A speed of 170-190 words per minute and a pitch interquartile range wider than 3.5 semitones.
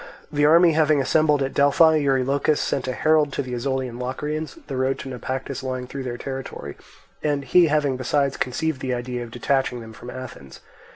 No: average, 185 wpm; average, 2.7 semitones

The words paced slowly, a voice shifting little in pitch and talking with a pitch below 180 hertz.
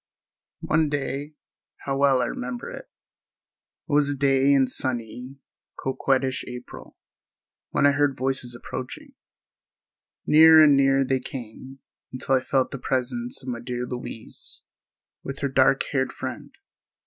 Yes: slow, 125 wpm; narrow, 1.7 semitones; low, 135 Hz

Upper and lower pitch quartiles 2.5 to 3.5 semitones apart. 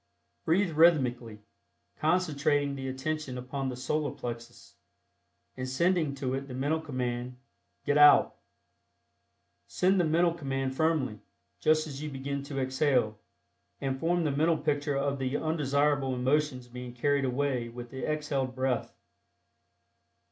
Yes: average, 3.0 semitones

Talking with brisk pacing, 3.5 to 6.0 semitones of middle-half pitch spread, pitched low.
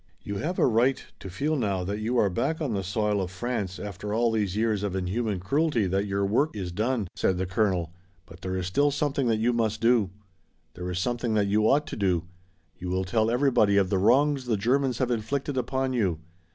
Yes: fast, 220 wpm; average, 4.5 semitones; low, 110 Hz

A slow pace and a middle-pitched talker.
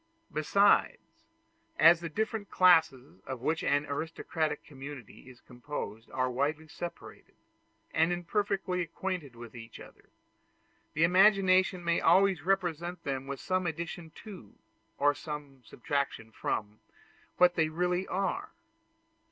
Yes: slow, 120 wpm; medium, 160 Hz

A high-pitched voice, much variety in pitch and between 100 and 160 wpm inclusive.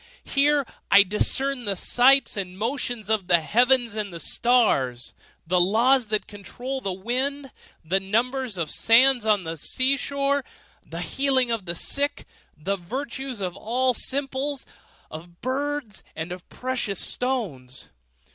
Yes: high, 230 Hz; wide, 6.0 semitones; average, 140 wpm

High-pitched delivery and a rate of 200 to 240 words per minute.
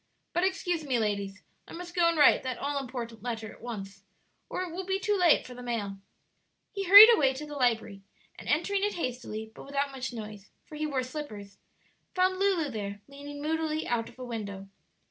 Yes: very high, 270 Hz; fast, 205 wpm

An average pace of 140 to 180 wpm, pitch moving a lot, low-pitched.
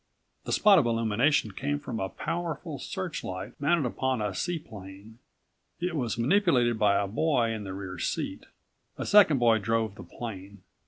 Yes: average, 160 wpm; wide, 6.5 semitones; low, 115 Hz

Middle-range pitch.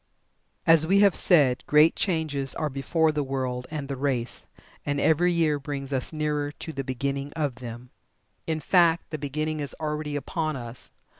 Yes: medium, 145 Hz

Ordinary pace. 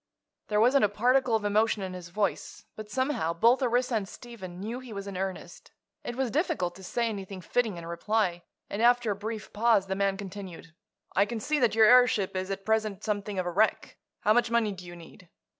No: fast, 215 wpm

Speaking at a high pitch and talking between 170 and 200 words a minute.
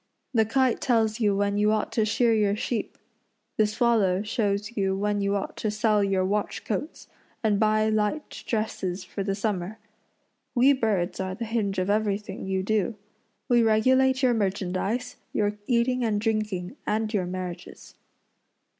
No: high, 210 Hz; average, 160 wpm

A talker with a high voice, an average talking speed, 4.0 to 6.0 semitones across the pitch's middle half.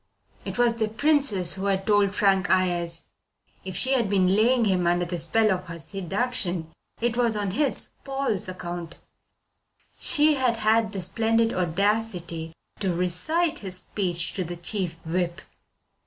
Yes: high, 195 Hz; average, 155 wpm; average, 4.4 semitones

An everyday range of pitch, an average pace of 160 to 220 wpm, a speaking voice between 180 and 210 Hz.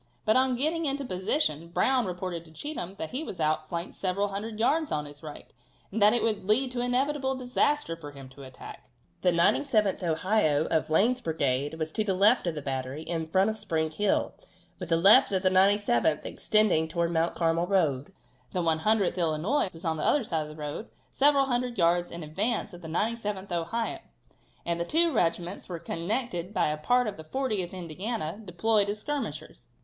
No: wide, 5.8 semitones; average, 195 wpm; medium, 185 Hz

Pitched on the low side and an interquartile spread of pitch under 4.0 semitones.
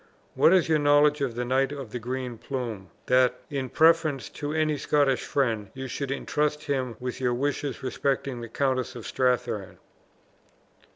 Yes: low, 130 Hz; average, 2.8 semitones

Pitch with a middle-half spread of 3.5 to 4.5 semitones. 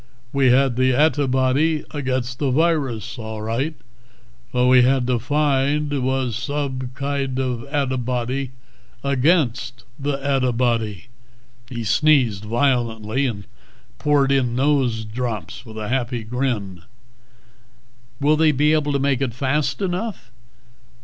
No: average, 2.9 semitones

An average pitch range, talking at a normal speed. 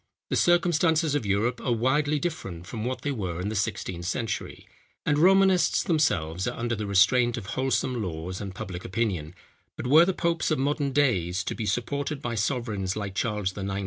No: wide, 6.8 semitones; average, 185 wpm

